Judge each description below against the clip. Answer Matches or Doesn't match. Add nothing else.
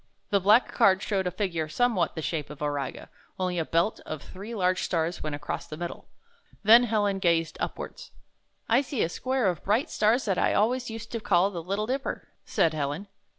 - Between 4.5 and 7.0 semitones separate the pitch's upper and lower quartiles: Matches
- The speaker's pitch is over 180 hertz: Matches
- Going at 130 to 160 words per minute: Doesn't match